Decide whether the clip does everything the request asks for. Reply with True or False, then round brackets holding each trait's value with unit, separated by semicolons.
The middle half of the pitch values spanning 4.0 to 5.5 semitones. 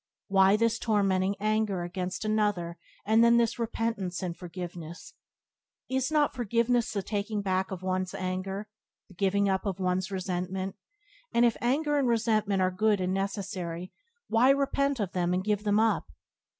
False (3.4 semitones)